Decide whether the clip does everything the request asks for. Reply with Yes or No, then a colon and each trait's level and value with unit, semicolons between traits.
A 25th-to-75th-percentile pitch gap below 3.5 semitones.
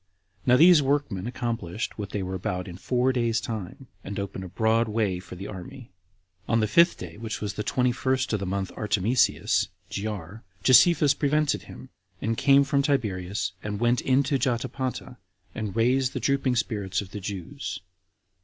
No: average, 4.8 semitones